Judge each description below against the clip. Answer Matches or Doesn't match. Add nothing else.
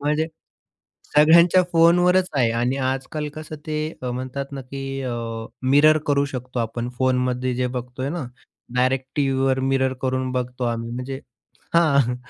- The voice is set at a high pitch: Doesn't match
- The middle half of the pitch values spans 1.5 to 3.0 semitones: Matches